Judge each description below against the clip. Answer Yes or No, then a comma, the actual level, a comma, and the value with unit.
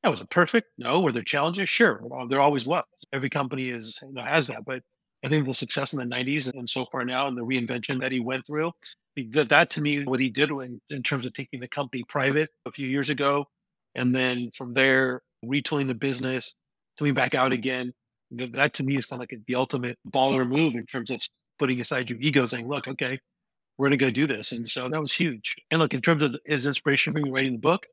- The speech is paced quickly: Yes, fast, 230 wpm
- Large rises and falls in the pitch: No, narrow, 2.4 semitones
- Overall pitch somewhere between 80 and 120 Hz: No, low, 135 Hz